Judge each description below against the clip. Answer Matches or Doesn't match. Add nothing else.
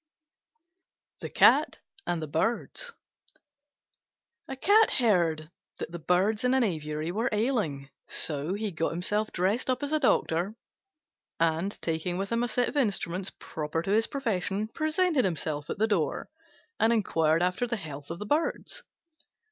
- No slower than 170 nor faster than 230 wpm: Doesn't match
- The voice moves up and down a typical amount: Doesn't match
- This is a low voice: Doesn't match